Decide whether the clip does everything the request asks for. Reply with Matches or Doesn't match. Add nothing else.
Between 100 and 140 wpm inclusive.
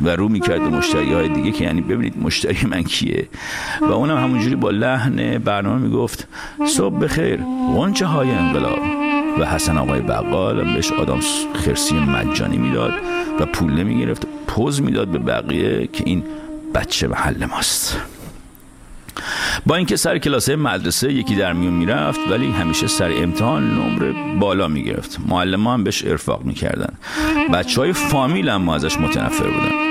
Doesn't match